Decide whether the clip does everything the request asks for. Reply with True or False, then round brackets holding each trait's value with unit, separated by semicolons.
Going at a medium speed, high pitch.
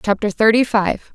True (155 wpm; 215 Hz)